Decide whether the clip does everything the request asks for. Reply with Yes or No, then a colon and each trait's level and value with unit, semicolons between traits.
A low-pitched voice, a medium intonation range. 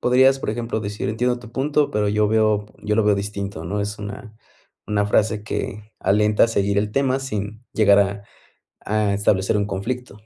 No: low, 105 Hz; narrow, 1.8 semitones